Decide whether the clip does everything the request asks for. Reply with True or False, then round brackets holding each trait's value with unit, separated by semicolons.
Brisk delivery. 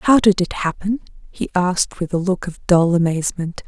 False (195 wpm)